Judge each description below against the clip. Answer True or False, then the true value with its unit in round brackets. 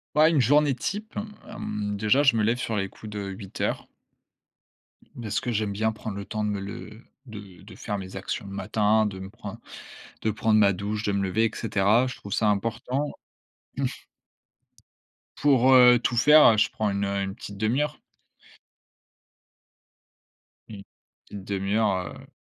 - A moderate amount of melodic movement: True (3.1 semitones)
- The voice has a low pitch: True (105 Hz)